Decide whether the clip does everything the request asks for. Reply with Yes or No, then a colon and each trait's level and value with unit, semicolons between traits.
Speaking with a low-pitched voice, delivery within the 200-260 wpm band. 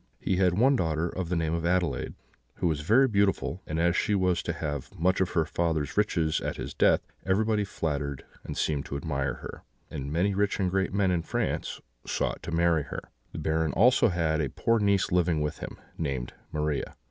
Yes: very low, 85 Hz; fast, 205 wpm